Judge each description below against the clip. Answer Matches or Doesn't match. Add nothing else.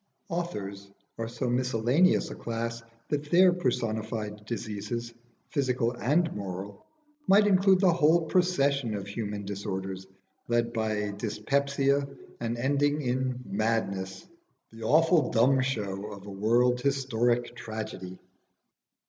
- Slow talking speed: Matches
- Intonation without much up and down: Doesn't match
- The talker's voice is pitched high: Doesn't match